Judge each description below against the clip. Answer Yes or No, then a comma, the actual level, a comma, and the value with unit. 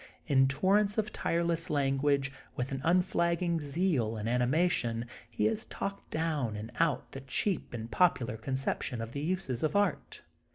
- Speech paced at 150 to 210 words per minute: Yes, average, 155 wpm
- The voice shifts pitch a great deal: Yes, wide, 5.8 semitones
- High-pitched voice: No, medium, 145 Hz